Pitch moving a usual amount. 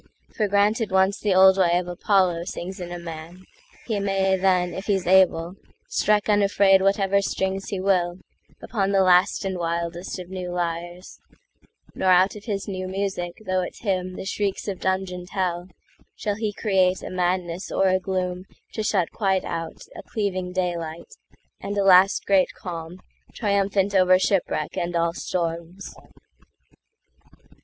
No: narrow, 1.7 semitones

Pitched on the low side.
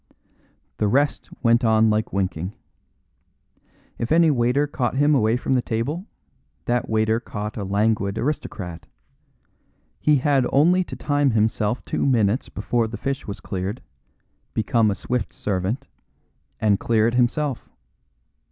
Yes: low, 115 Hz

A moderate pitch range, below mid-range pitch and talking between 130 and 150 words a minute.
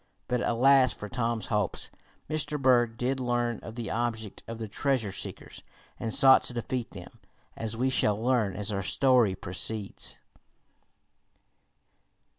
Yes: average, 3.0 semitones; low, 120 Hz; average, 140 wpm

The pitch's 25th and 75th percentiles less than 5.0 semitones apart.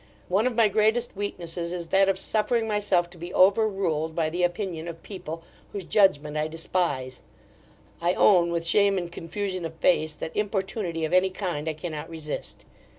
Yes: average, 3.4 semitones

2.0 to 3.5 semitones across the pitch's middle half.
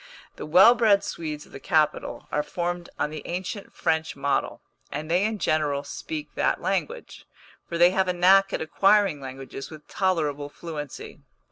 No: average, 4.4 semitones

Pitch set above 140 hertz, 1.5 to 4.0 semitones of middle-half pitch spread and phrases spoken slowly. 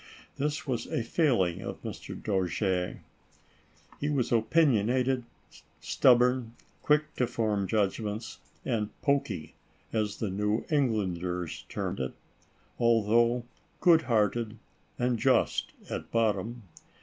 No: low, 115 Hz; average, 3.4 semitones; slow, 105 wpm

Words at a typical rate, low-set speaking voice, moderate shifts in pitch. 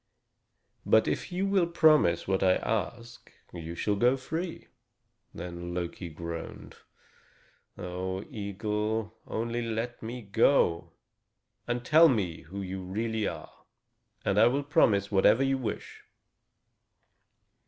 No: slow, 120 wpm; low, 110 Hz; average, 4.8 semitones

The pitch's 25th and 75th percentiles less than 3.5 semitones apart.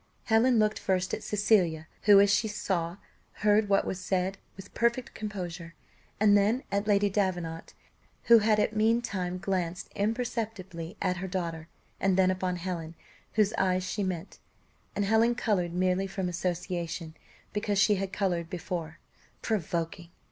Yes: average, 2.8 semitones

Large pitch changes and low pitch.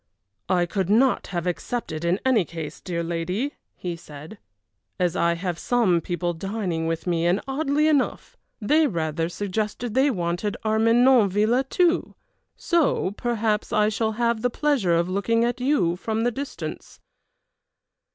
No: wide, 5.9 semitones; high, 210 Hz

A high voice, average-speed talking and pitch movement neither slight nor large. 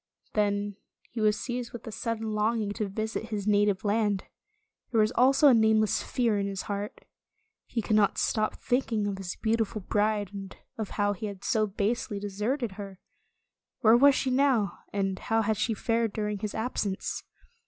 No: high, 215 Hz; average, 185 wpm; narrow, 2.0 semitones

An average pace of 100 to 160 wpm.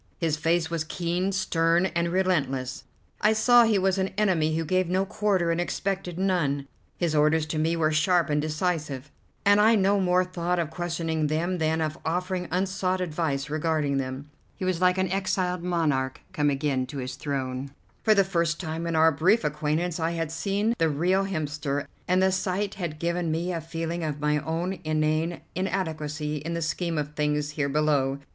No: average, 185 wpm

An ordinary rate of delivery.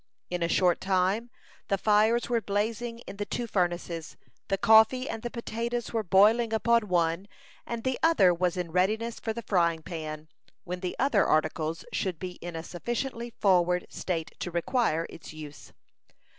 Yes: average, 170 wpm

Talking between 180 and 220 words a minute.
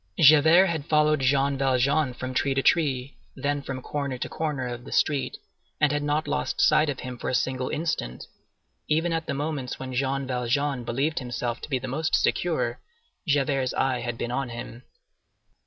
Yes: average, 185 wpm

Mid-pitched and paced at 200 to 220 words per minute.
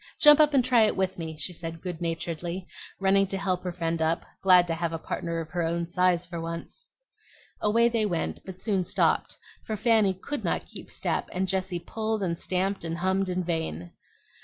Yes: medium, 180 Hz; fast, 205 wpm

